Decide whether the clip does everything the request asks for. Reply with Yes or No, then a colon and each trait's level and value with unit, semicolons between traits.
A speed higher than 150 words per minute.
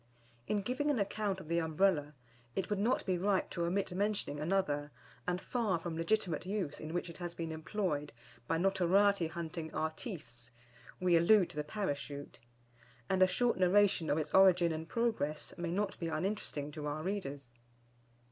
Yes: average, 170 wpm